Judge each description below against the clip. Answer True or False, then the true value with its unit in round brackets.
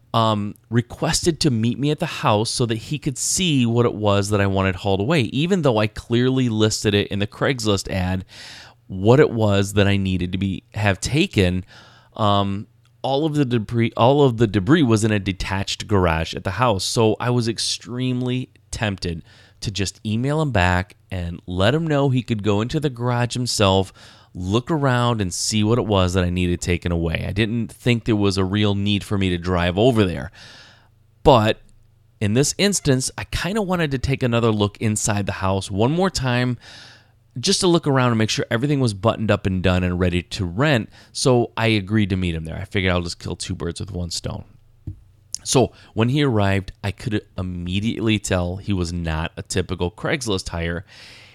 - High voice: False (110 Hz)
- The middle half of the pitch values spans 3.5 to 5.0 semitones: True (3.8 semitones)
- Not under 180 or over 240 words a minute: True (200 wpm)